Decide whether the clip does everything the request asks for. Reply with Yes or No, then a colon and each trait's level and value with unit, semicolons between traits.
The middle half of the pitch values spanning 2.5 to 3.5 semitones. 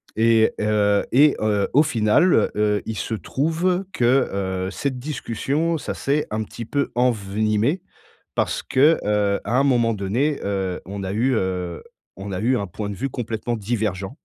No: average, 4.8 semitones